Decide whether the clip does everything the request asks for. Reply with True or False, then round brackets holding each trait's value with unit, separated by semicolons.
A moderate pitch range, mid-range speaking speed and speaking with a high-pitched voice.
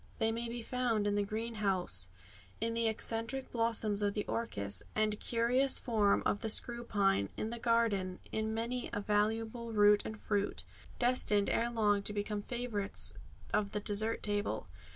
False (2.2 semitones; 165 wpm; 220 Hz)